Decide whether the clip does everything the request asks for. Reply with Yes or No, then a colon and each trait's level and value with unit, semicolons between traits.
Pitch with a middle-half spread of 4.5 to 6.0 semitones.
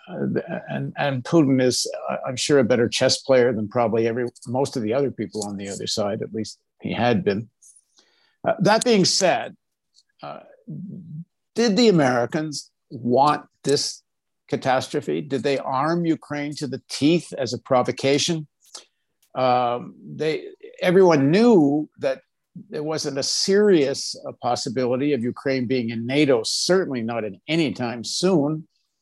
Yes: average, 5.0 semitones